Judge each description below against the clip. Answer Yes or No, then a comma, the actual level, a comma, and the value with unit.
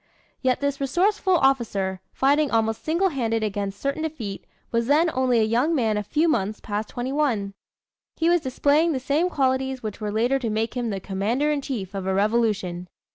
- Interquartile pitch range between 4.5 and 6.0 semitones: Yes, average, 5.1 semitones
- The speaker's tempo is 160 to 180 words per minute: No, average, 190 wpm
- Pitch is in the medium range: No, high, 245 Hz